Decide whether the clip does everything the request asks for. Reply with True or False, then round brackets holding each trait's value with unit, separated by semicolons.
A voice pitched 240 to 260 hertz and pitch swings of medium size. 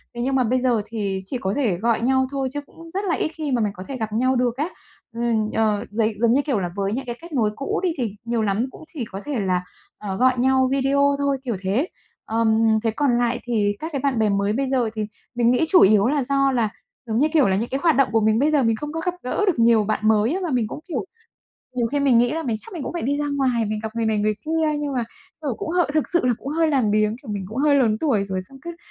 True (245 Hz; 4.4 semitones)